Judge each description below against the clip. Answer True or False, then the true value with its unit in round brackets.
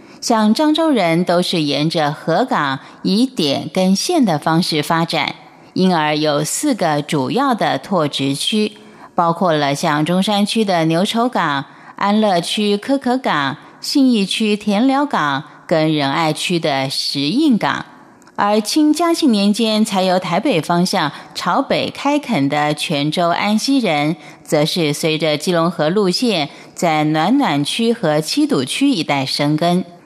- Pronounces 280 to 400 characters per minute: False (210 characters per minute)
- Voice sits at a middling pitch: True (175 Hz)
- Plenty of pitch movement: True (6.6 semitones)